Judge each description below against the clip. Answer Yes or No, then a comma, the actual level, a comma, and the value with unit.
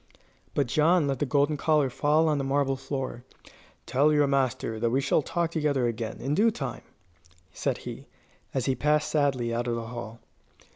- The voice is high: No, low, 135 Hz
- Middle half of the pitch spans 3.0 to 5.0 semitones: Yes, average, 3.4 semitones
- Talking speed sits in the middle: Yes, average, 185 wpm